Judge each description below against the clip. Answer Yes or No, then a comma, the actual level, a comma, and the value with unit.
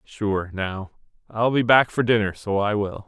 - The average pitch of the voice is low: Yes, low, 105 Hz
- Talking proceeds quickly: No, average, 195 wpm